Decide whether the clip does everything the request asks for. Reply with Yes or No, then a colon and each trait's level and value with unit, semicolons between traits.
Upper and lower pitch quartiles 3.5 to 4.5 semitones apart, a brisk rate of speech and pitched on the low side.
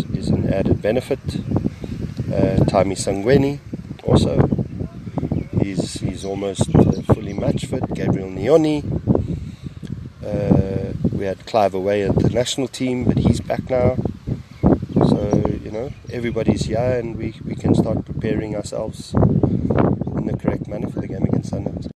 No: average, 4.0 semitones; average, 140 wpm; low, 115 Hz